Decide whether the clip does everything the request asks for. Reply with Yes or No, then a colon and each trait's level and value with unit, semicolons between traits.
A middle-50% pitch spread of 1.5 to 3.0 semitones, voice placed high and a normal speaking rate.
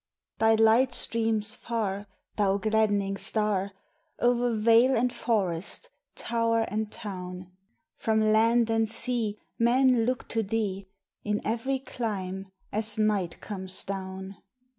No: narrow, 2.6 semitones; high, 220 Hz; slow, 120 wpm